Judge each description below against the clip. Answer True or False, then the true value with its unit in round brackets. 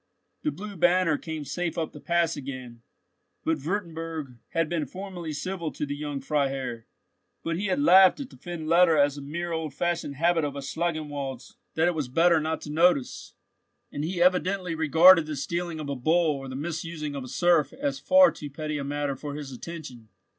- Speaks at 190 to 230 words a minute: True (195 wpm)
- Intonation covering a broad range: False (3.3 semitones)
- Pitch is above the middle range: False (160 Hz)